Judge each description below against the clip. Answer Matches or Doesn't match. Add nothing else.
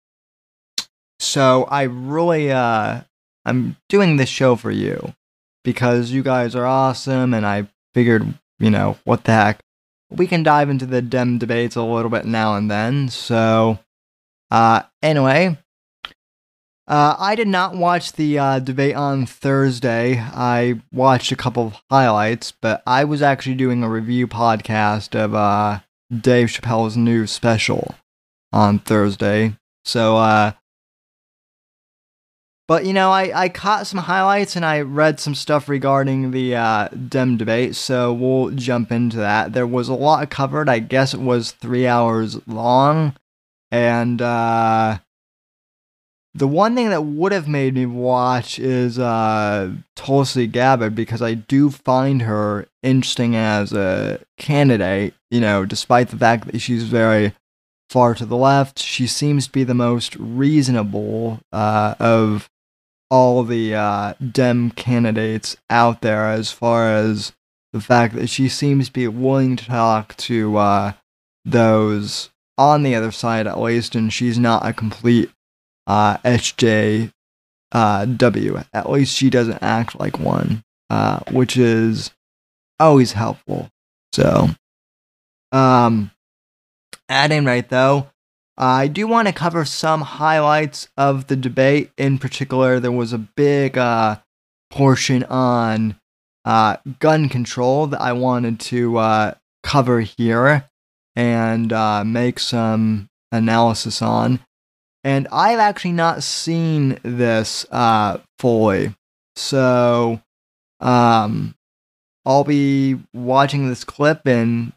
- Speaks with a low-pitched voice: Matches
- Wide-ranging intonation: Doesn't match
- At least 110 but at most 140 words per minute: Matches